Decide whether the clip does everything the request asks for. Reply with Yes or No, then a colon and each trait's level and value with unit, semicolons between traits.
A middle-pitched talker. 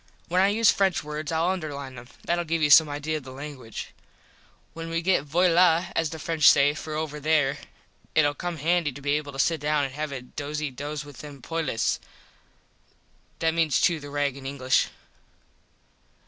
Yes: medium, 150 Hz